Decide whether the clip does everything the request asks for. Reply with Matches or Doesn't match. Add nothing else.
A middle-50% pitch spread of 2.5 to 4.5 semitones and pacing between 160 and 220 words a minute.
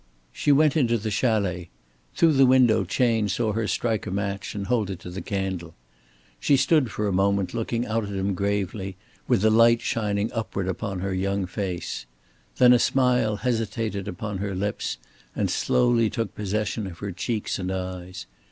Matches